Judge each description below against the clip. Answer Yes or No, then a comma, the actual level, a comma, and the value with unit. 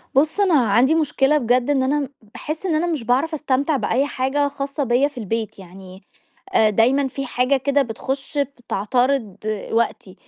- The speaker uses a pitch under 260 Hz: No, very high, 270 Hz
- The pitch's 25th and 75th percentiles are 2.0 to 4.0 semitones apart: Yes, average, 3.3 semitones